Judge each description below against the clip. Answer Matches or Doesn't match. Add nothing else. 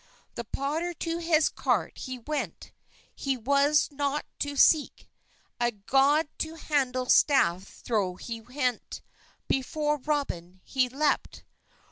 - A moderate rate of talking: Doesn't match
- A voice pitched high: Matches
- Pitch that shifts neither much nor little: Matches